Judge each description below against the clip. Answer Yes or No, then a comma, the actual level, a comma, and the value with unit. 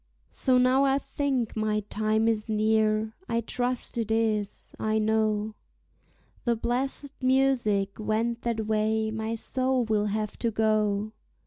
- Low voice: No, high, 220 Hz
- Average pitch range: No, narrow, 2.0 semitones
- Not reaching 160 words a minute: Yes, slow, 135 wpm